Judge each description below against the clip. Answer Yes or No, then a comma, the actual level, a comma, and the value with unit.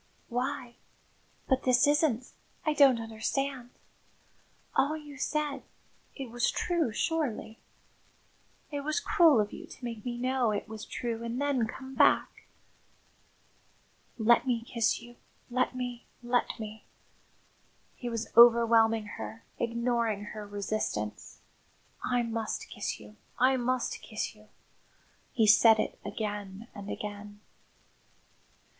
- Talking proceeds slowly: Yes, slow, 125 wpm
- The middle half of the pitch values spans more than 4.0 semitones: No, average, 3.0 semitones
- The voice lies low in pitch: No, high, 235 Hz